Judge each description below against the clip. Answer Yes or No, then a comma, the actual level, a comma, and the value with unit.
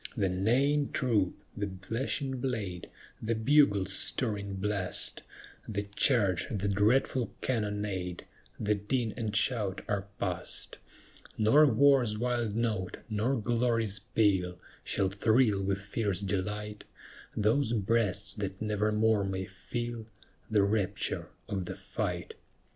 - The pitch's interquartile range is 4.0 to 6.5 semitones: No, average, 3.0 semitones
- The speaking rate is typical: No, slow, 115 wpm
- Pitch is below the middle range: Yes, low, 105 Hz